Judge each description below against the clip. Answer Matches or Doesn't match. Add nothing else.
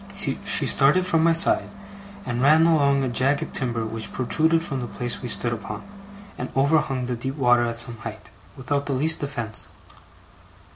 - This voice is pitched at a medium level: Doesn't match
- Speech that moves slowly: Doesn't match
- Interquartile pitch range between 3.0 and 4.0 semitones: Matches